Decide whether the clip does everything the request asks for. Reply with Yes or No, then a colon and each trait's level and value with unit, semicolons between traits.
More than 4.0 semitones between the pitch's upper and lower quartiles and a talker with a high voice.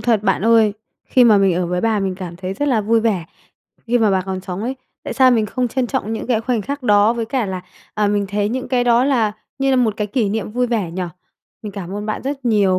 No: average, 3.7 semitones; high, 220 Hz